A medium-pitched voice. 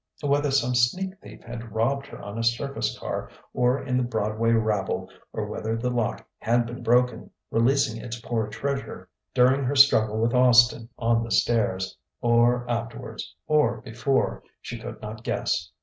No: low, 120 Hz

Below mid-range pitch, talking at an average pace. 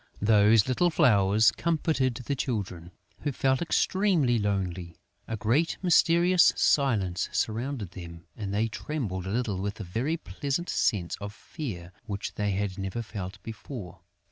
Yes: low, 110 Hz; average, 145 wpm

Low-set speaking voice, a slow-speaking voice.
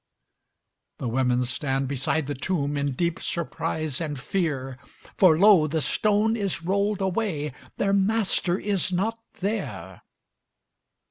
No: medium, 170 Hz; slow, 125 wpm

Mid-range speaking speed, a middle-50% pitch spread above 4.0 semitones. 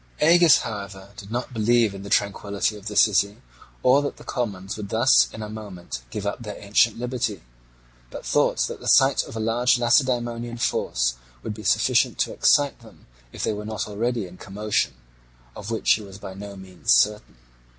No: average, 190 wpm; average, 3.0 semitones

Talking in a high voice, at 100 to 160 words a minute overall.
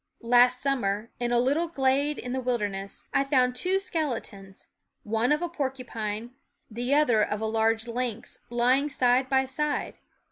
Yes: very high, 250 Hz; average, 155 wpm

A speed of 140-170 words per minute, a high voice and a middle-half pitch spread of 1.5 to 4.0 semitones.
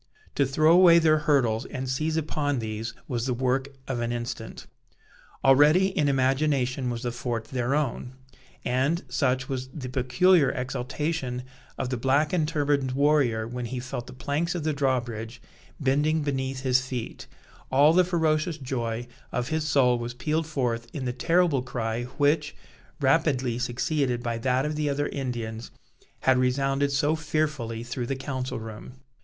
No: average, 160 wpm; low, 135 Hz; average, 3.4 semitones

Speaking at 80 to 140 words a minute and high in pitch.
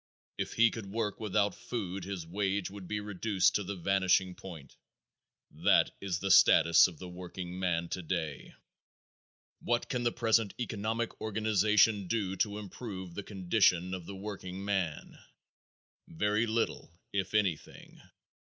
No: slow, 135 wpm; low, 100 Hz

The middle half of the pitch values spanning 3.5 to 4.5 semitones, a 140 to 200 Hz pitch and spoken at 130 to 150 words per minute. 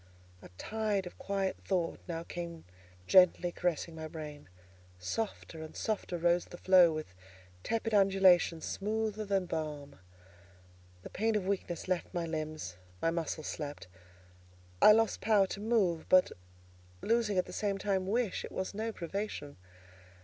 Yes: average, 3.9 semitones; medium, 185 Hz; average, 145 wpm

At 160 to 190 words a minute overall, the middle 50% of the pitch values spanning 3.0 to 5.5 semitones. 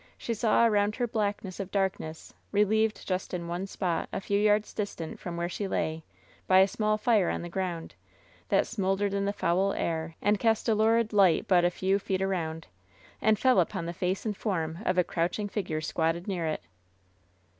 No: average, 200 wpm; average, 3.4 semitones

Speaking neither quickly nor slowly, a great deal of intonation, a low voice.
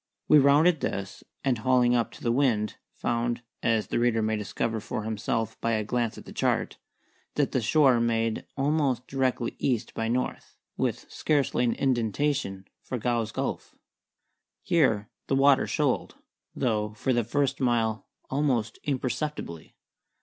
No: average, 150 wpm; average, 3.3 semitones; low, 120 Hz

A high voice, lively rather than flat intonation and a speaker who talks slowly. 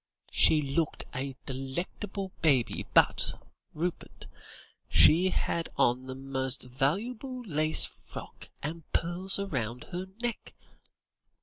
No: medium, 155 Hz; wide, 5.9 semitones; slow, 105 wpm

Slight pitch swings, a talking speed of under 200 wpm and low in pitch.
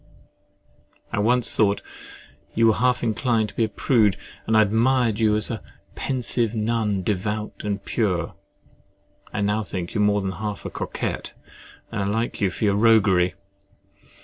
Yes: narrow, 2.0 semitones; average, 165 wpm; low, 110 Hz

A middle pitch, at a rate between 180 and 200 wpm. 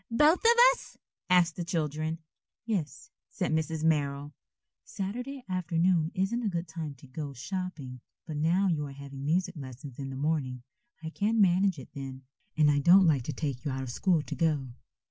Yes: medium, 160 Hz; average, 185 wpm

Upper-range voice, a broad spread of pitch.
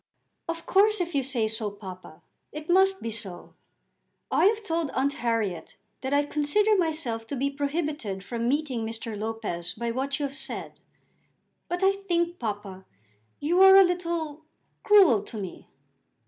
Yes: very high, 280 Hz; wide, 7.4 semitones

